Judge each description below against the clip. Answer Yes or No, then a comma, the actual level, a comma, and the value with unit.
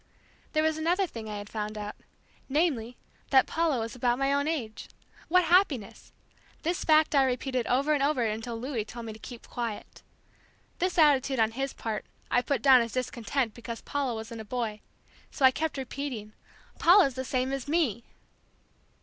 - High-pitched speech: Yes, very high, 255 Hz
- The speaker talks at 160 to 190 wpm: Yes, average, 175 wpm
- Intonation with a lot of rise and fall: No, average, 4.3 semitones